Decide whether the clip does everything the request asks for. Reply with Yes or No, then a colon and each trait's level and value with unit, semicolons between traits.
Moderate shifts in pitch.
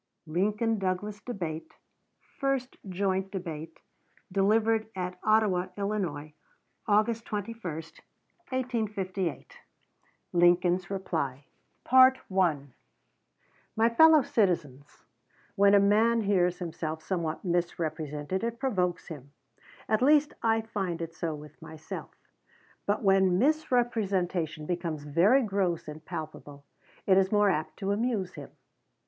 Yes: average, 4.6 semitones